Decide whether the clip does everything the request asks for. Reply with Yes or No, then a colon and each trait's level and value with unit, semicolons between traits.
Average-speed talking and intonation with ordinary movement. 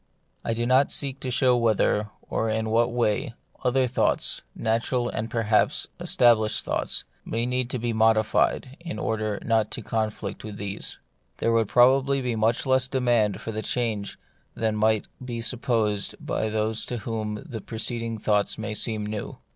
No: average, 165 wpm; narrow, 2.3 semitones